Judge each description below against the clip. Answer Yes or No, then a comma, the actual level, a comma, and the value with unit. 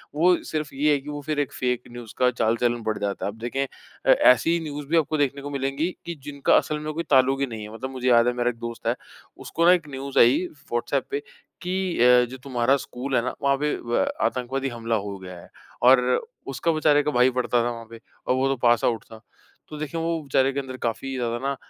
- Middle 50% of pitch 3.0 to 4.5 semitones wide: Yes, average, 3.6 semitones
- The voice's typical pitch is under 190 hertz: Yes, low, 135 Hz